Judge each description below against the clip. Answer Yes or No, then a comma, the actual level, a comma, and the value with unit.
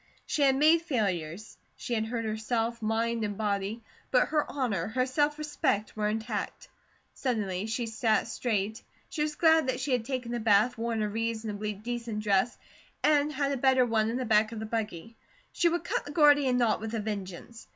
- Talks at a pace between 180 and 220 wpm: Yes, average, 195 wpm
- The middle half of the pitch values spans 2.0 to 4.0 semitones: Yes, average, 3.4 semitones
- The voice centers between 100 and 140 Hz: No, high, 230 Hz